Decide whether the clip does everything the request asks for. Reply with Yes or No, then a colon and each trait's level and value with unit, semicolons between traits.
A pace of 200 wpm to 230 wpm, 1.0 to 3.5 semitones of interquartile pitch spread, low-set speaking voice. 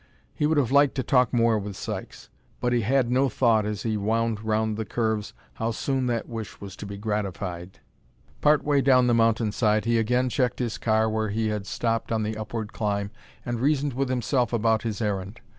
Yes: fast, 205 wpm; average, 2.7 semitones; low, 115 Hz